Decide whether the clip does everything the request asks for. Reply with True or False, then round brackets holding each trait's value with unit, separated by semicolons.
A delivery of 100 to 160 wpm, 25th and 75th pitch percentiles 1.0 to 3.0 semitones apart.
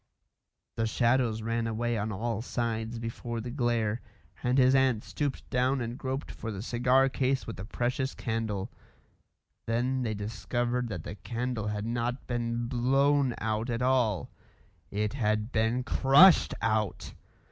True (145 wpm; 2.4 semitones)